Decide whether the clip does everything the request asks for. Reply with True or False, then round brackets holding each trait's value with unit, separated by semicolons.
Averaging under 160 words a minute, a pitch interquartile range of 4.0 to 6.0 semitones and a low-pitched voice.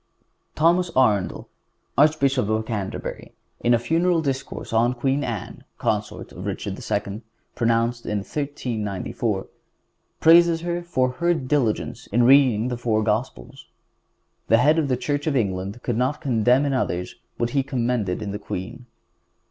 True (145 wpm; 4.6 semitones; 125 Hz)